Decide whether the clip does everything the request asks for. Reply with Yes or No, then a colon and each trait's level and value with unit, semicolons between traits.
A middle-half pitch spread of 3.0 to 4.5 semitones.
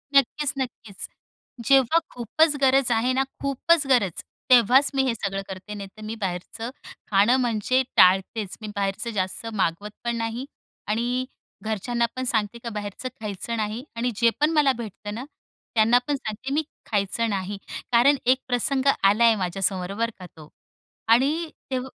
Yes: average, 4.0 semitones